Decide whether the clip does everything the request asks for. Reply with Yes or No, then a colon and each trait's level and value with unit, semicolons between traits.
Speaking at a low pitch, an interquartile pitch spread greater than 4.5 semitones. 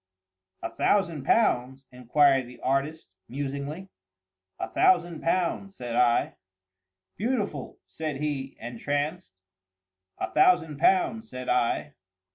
No: medium, 145 Hz; wide, 5.4 semitones